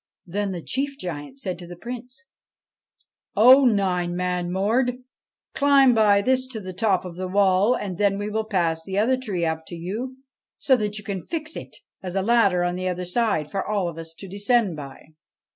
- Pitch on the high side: Yes, high, 200 Hz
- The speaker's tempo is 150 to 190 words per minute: No, average, 200 wpm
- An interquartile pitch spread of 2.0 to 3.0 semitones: No, average, 4.9 semitones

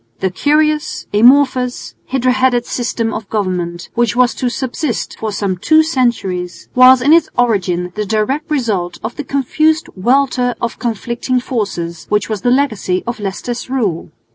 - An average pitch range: Yes, average, 4.3 semitones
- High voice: Yes, high, 240 Hz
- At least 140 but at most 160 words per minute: Yes, average, 155 wpm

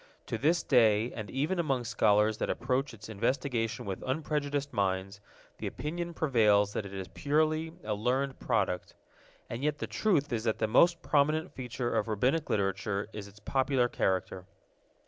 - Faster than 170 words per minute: No, average, 165 wpm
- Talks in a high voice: No, low, 120 Hz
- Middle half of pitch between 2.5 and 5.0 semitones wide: No, wide, 5.5 semitones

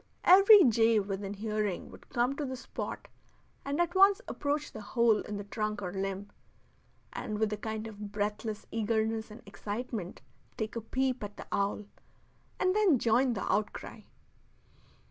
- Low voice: No, high, 220 Hz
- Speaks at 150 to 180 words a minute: Yes, average, 160 wpm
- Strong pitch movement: No, average, 3.7 semitones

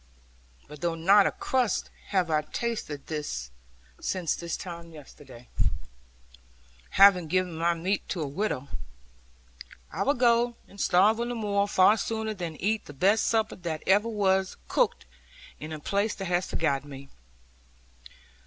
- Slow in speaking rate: No, average, 145 wpm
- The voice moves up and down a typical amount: Yes, average, 4.8 semitones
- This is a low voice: No, medium, 185 Hz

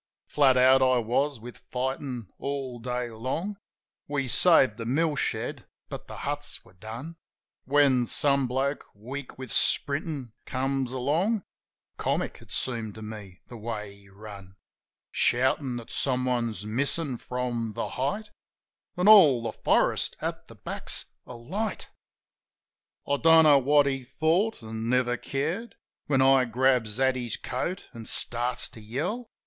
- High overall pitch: No, low, 130 Hz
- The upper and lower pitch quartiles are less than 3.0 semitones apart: No, average, 3.4 semitones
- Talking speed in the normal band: Yes, average, 145 wpm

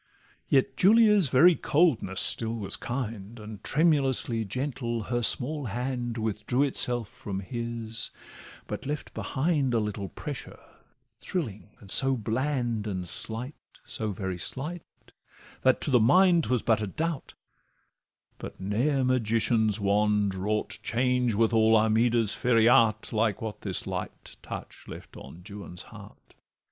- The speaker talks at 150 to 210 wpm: No, slow, 135 wpm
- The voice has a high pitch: No, low, 115 Hz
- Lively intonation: No, average, 3.8 semitones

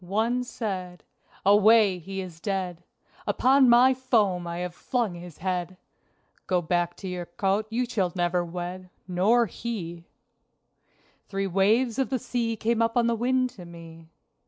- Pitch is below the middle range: No, high, 195 Hz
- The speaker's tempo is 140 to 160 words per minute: Yes, average, 155 wpm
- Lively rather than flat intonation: No, average, 4.7 semitones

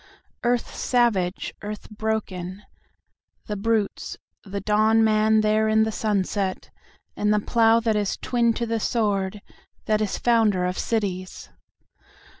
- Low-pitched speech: No, high, 215 Hz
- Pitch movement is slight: Yes, narrow, 2.0 semitones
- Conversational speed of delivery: No, slow, 125 wpm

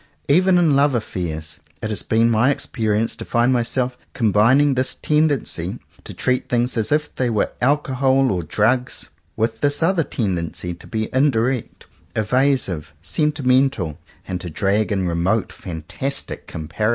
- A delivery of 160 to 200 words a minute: No, average, 150 wpm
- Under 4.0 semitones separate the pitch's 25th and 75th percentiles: No, wide, 5.5 semitones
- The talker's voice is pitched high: No, low, 120 Hz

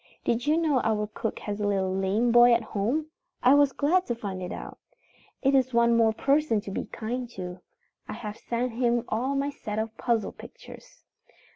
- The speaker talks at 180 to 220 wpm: Yes, average, 195 wpm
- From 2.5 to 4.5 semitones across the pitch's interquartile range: Yes, average, 3.6 semitones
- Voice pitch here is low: No, high, 235 Hz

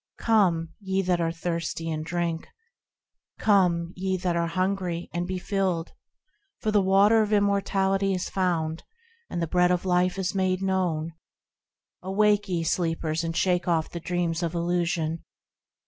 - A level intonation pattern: Yes, narrow, 2.3 semitones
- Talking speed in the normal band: Yes, average, 145 wpm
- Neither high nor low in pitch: Yes, medium, 180 Hz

